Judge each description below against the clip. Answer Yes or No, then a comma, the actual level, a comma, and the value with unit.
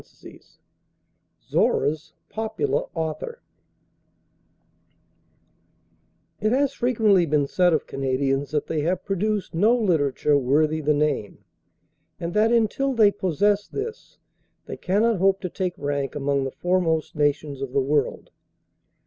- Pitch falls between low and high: Yes, medium, 165 Hz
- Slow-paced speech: Yes, slow, 125 wpm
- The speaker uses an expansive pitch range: Yes, wide, 6.3 semitones